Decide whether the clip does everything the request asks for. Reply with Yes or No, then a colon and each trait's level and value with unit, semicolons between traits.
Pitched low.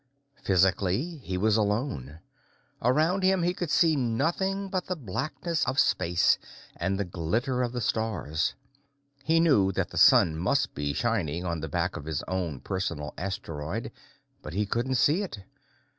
Yes: low, 105 Hz